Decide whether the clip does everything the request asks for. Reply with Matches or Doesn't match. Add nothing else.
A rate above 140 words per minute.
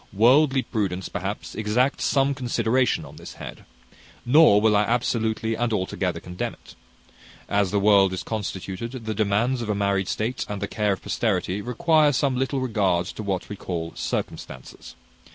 Matches